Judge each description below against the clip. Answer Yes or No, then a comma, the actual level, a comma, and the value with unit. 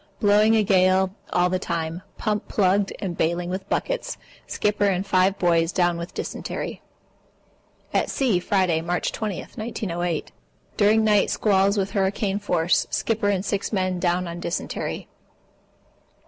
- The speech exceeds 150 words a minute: No, average, 145 wpm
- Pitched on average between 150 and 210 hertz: Yes, high, 190 Hz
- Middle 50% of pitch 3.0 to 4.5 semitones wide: No, narrow, 2.5 semitones